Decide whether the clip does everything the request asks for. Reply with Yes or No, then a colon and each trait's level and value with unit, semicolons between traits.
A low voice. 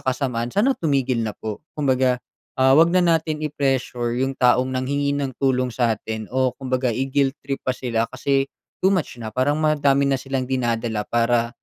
Yes: low, 130 Hz